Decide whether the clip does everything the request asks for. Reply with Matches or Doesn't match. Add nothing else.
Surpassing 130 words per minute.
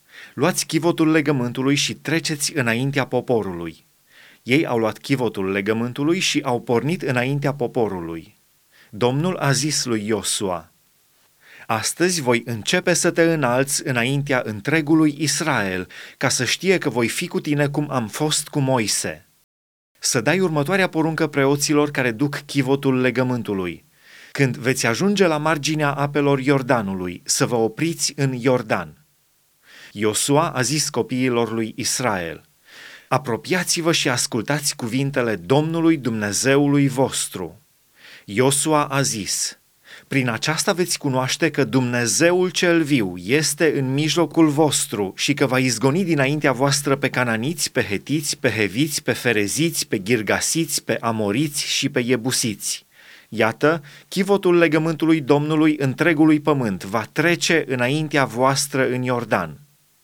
Doesn't match